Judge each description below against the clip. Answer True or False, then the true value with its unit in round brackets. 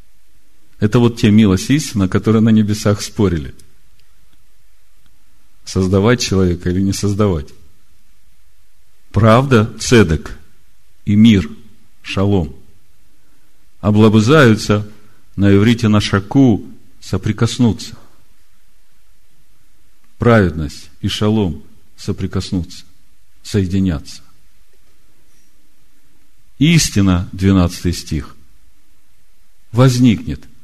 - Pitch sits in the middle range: False (100 Hz)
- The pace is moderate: False (65 wpm)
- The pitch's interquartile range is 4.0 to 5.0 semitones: False (3.2 semitones)